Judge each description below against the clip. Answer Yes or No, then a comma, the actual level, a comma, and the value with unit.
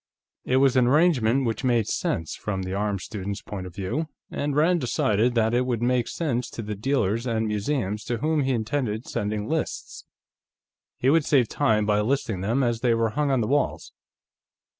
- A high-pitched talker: No, low, 120 Hz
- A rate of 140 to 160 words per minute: No, average, 190 wpm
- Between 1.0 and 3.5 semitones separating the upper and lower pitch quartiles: No, average, 4.2 semitones